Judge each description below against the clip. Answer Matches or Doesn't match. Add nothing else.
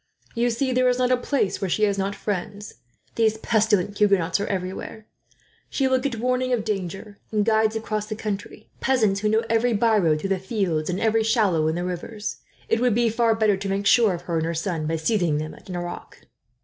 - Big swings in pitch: Doesn't match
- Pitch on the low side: Doesn't match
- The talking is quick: Matches